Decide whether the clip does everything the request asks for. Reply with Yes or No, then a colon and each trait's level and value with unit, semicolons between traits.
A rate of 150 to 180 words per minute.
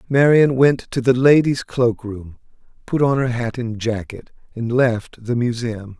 Yes: average, 170 wpm